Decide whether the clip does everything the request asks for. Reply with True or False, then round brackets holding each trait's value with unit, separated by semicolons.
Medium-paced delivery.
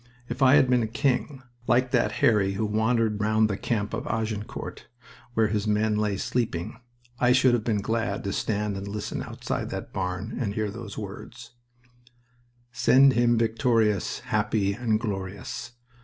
True (155 wpm)